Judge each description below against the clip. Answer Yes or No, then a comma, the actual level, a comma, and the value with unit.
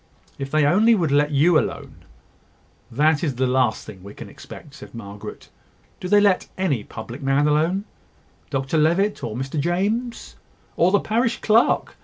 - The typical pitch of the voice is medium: Yes, medium, 150 Hz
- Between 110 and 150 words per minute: No, average, 170 wpm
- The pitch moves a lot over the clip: Yes, wide, 5.9 semitones